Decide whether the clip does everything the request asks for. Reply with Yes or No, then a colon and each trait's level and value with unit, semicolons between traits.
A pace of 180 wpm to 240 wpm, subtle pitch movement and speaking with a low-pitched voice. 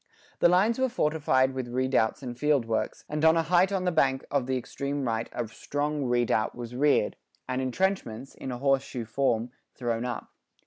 No: average, 190 wpm; average, 3.8 semitones; low, 130 Hz